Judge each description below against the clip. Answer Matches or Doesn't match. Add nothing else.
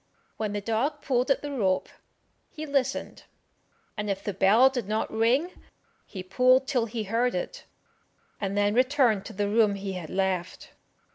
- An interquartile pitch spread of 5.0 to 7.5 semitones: Doesn't match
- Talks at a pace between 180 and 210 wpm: Doesn't match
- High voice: Matches